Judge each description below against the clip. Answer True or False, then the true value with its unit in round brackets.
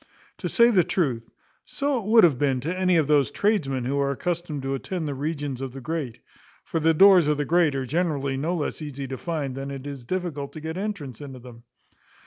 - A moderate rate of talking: False (225 wpm)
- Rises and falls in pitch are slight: False (4.4 semitones)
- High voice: False (150 Hz)